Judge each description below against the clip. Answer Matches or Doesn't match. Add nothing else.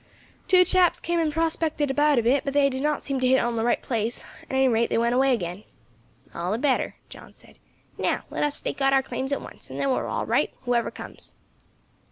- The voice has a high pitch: Matches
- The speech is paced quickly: Matches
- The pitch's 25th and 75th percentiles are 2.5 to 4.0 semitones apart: Matches